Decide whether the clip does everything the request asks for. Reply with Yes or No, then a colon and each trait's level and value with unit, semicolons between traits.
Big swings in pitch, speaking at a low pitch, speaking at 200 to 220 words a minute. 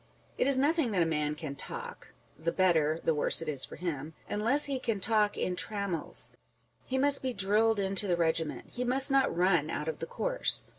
No: wide, 7.7 semitones; high, 195 Hz; fast, 205 wpm